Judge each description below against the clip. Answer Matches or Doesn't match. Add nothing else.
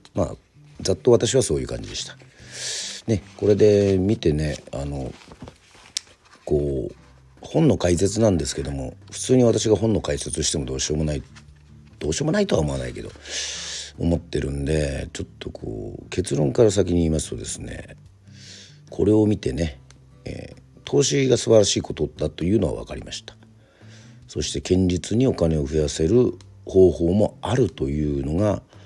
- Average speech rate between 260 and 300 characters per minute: Doesn't match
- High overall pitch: Doesn't match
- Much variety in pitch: Matches